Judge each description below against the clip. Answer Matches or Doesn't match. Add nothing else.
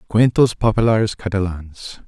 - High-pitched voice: Doesn't match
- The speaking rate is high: Doesn't match